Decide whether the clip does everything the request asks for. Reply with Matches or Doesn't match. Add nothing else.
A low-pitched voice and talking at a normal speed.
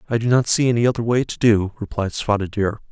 Doesn't match